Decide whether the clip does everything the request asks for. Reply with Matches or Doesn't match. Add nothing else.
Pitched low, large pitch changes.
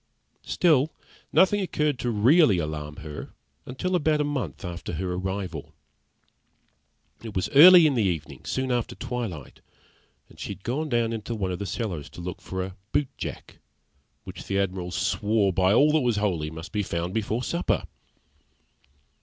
Matches